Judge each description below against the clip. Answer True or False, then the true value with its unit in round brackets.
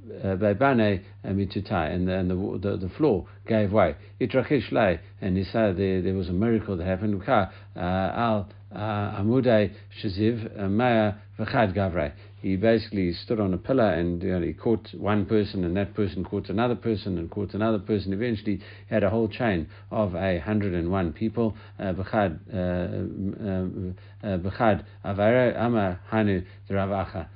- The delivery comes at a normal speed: False (130 wpm)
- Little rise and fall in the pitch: True (2.3 semitones)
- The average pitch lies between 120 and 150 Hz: False (100 Hz)